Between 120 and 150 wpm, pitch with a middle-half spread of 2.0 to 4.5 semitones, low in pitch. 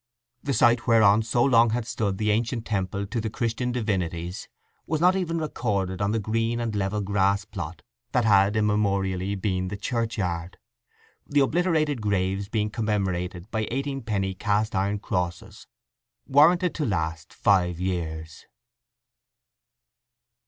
Yes: average, 140 wpm; average, 3.6 semitones; low, 105 Hz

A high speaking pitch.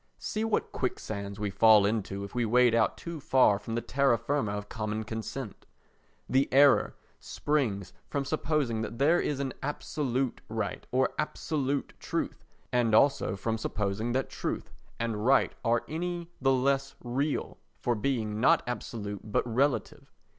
No: low, 120 Hz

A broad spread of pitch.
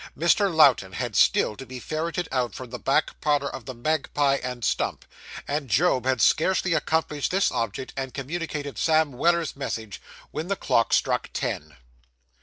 No: average, 3.9 semitones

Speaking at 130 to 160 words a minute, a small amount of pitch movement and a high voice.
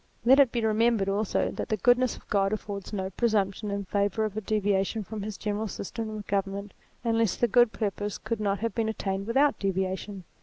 No: average, 200 wpm; narrow, 2.3 semitones; high, 210 Hz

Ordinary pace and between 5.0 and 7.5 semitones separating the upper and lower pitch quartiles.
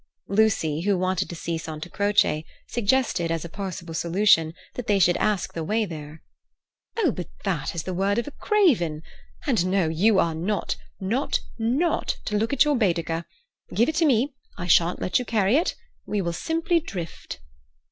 Yes: average, 180 wpm; average, 5.3 semitones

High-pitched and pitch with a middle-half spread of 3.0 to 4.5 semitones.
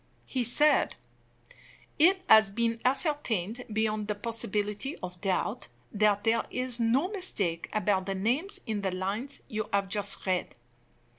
Yes: high, 215 Hz; average, 4.0 semitones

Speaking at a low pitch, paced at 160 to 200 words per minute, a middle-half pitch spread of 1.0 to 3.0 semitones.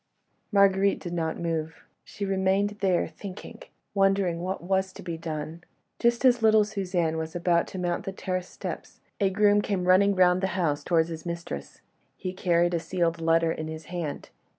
No: medium, 180 Hz; average, 175 wpm; average, 2.7 semitones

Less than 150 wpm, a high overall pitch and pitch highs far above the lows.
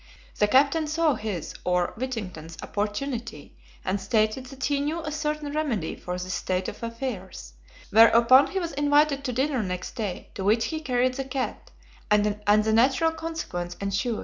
No: average, 165 wpm; high, 240 Hz; wide, 5.9 semitones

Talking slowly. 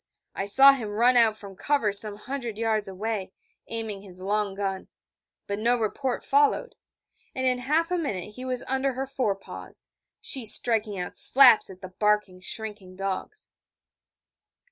No: average, 160 wpm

